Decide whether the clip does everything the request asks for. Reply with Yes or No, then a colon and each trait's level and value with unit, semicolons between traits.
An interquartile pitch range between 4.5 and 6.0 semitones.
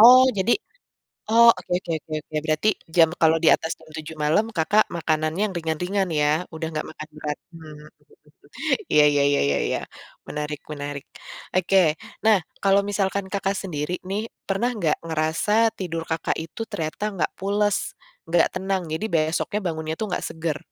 No: average, 3.9 semitones